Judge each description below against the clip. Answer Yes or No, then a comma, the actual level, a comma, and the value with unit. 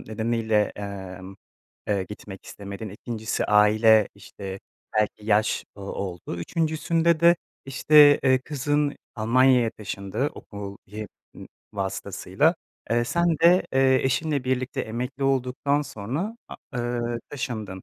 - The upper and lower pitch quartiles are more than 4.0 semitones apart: Yes, average, 5.1 semitones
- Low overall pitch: Yes, low, 115 Hz